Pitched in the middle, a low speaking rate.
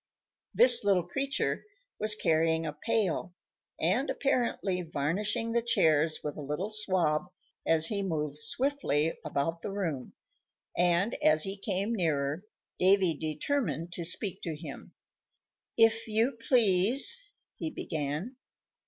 Yes: medium, 180 Hz; slow, 125 wpm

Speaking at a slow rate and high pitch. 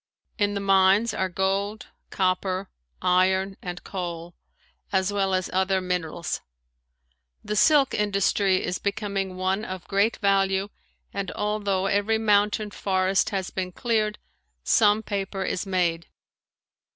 Yes: slow, 125 wpm; high, 195 Hz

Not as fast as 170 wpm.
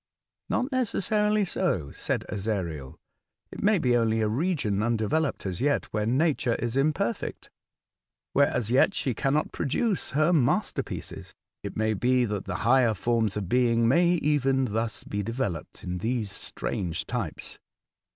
Yes: average, 155 wpm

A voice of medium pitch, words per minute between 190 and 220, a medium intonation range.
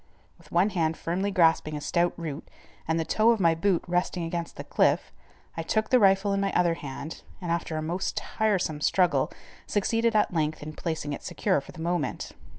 Yes: medium, 170 Hz; average, 200 wpm; average, 3.4 semitones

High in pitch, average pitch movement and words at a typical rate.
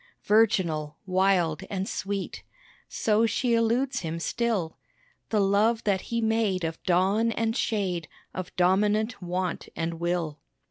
No: high, 195 Hz; average, 4.1 semitones; slow, 130 wpm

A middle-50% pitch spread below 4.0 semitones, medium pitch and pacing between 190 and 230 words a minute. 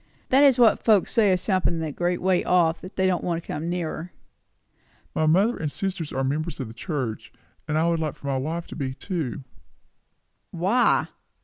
Yes: average, 3.5 semitones; medium, 170 Hz; average, 200 wpm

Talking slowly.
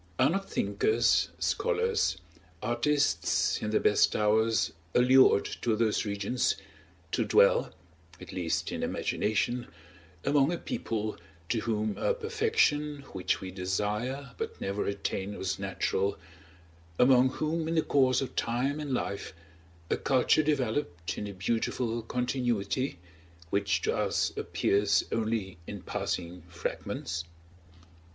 Yes: slow, 125 wpm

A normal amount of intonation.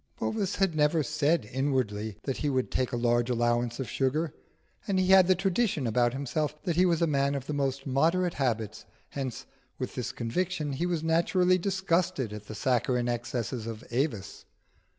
No: wide, 5.9 semitones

